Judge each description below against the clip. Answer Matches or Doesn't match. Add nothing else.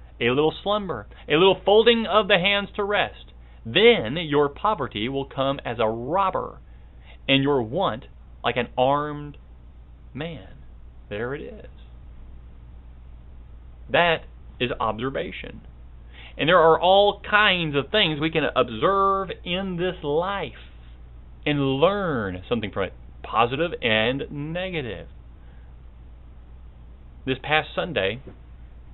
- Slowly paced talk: Matches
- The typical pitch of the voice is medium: Doesn't match